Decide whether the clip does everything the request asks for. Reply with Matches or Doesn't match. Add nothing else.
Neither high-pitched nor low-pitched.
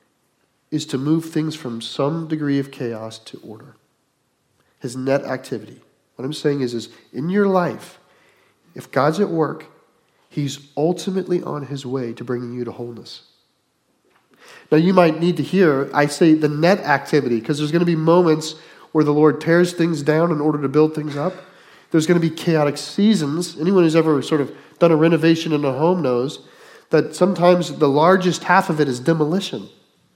Matches